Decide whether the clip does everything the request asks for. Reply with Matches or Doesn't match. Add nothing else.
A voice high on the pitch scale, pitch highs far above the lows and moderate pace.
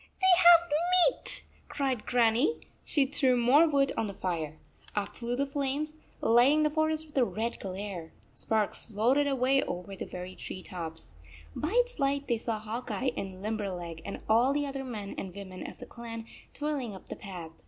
Matches